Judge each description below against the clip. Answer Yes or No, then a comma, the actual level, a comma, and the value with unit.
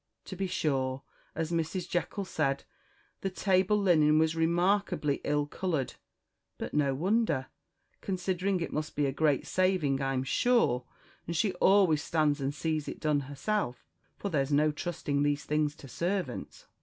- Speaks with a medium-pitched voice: Yes, medium, 155 Hz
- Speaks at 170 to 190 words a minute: No, average, 155 wpm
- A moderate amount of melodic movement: Yes, average, 4.5 semitones